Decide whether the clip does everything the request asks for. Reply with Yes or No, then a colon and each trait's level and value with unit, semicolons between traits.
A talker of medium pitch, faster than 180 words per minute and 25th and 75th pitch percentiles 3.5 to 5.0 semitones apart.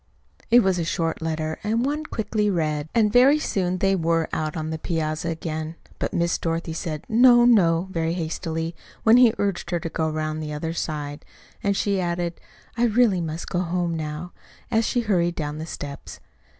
Yes: medium, 170 Hz; average, 190 wpm; average, 4.2 semitones